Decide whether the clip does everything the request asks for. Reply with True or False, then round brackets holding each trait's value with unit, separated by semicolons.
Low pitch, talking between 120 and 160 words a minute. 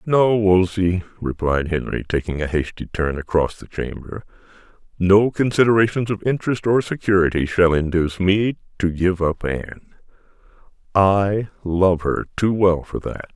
True (95 Hz; 140 wpm)